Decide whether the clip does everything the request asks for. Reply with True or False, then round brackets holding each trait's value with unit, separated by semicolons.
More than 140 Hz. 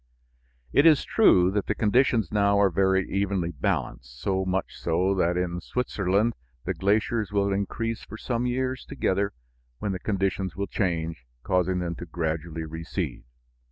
False (95 Hz)